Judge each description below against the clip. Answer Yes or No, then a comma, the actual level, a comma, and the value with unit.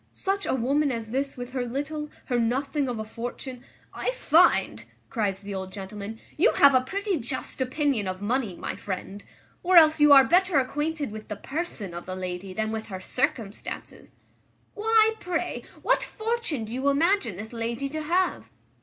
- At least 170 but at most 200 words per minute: Yes, average, 180 wpm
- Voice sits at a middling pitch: No, very high, 260 Hz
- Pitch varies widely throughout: Yes, wide, 6.1 semitones